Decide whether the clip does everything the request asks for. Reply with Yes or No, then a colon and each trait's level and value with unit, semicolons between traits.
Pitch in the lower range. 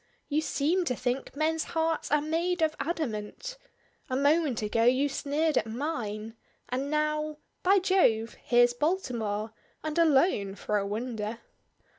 No: very high, 285 Hz